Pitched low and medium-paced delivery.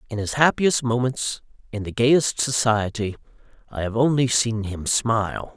Yes: low, 115 Hz; average, 150 wpm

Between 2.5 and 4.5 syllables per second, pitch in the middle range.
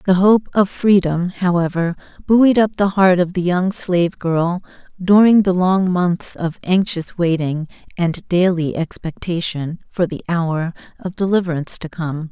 Yes: 4.3 syllables/s; medium, 180 Hz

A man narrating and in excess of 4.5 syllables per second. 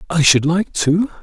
No: male; 4.4 syllables/s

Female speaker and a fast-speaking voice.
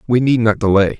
No: male; fast, 240 wpm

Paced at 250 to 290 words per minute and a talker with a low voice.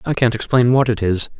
Yes: fast, 260 wpm; low, 115 Hz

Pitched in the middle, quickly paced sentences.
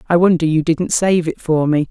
Yes: medium, 165 Hz; fast, 250 wpm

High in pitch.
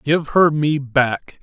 No: medium, 145 Hz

